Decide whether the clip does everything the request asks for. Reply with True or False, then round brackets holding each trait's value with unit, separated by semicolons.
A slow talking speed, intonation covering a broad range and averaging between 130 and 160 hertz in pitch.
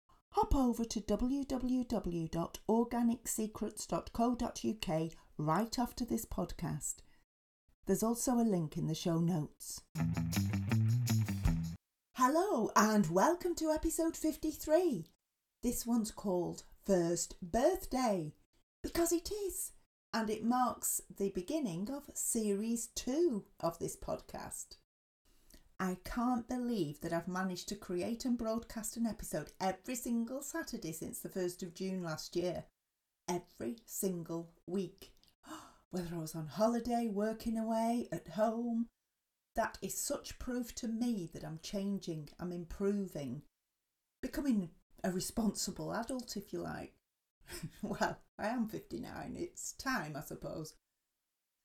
False (115 wpm; 5.9 semitones; 205 Hz)